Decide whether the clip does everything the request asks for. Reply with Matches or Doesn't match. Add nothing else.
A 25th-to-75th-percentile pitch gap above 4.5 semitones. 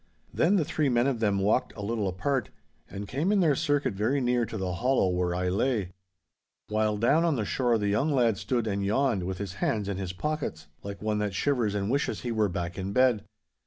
Matches